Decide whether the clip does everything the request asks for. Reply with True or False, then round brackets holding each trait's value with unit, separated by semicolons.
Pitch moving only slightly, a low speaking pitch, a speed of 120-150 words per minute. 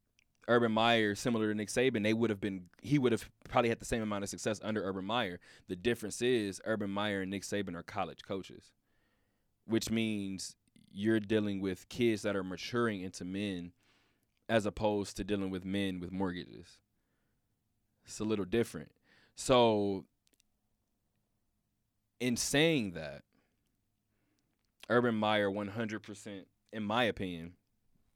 True (2.3 semitones; 105 Hz; 145 wpm)